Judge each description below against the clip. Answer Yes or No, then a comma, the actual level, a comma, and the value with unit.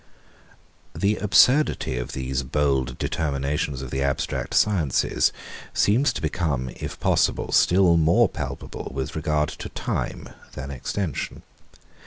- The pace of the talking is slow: Yes, slow, 120 wpm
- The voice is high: No, very low, 75 Hz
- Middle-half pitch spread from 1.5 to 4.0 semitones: No, average, 4.8 semitones